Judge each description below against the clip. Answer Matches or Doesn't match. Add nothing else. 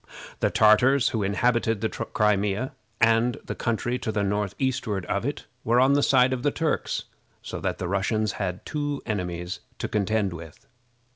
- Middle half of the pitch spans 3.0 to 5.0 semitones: Matches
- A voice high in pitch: Doesn't match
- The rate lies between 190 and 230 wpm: Doesn't match